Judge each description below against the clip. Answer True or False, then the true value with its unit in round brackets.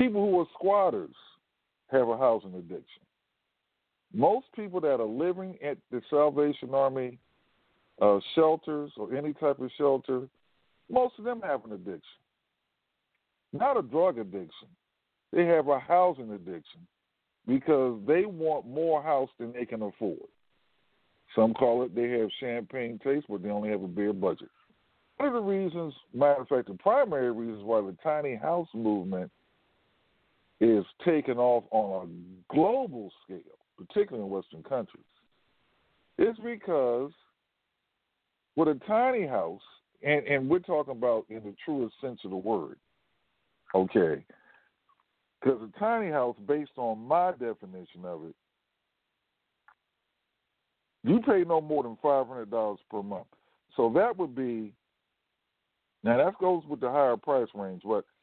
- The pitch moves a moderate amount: False (6.6 semitones)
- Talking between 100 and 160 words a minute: True (145 wpm)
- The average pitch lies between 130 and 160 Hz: True (135 Hz)